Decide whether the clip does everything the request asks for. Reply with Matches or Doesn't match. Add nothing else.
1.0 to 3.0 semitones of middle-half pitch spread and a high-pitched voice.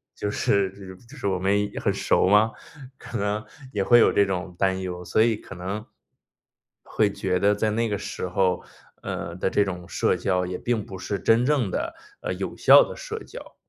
Doesn't match